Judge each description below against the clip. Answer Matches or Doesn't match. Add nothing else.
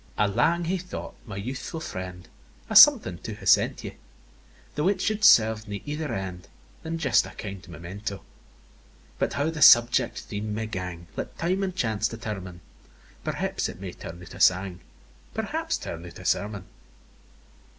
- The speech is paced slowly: Doesn't match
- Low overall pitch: Matches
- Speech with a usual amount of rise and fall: Doesn't match